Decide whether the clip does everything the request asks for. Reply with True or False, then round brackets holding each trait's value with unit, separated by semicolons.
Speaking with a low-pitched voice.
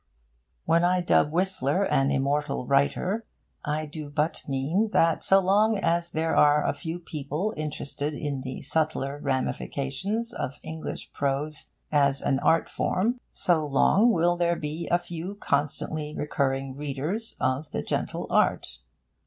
False (150 Hz)